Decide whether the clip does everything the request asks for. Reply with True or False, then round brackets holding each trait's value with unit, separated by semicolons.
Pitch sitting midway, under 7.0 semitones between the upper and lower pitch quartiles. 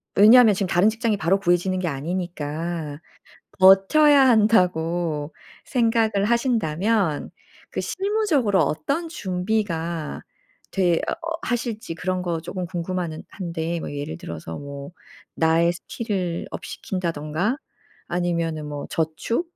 True (180 Hz; 5.1 semitones)